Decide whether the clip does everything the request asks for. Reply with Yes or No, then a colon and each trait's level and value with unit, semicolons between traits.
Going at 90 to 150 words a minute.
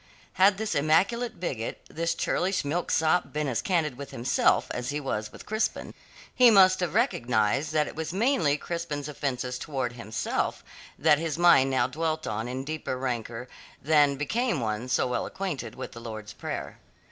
No: average, 170 wpm